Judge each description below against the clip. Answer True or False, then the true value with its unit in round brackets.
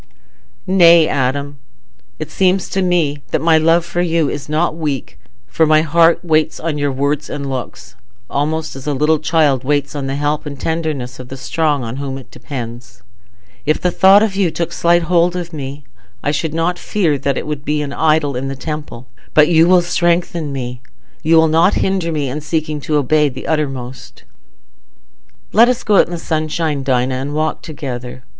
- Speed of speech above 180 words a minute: True (190 wpm)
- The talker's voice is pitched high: False (150 Hz)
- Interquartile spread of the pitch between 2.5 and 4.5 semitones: True (3.1 semitones)